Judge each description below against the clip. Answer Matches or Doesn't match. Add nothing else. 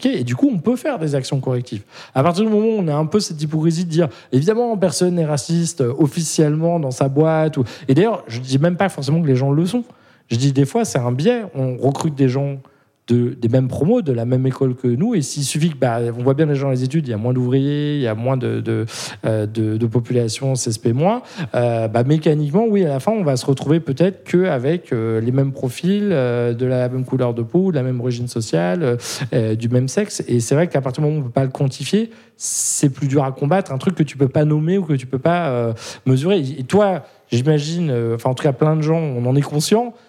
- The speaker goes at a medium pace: Doesn't match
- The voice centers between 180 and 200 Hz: Doesn't match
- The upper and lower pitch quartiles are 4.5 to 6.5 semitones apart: Matches